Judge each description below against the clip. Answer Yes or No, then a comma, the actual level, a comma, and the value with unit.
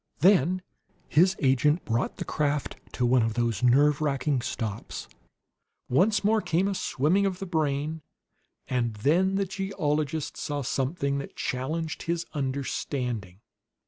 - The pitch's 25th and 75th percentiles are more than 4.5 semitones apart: Yes, average, 5.2 semitones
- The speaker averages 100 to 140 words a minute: Yes, slow, 135 wpm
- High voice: No, medium, 145 Hz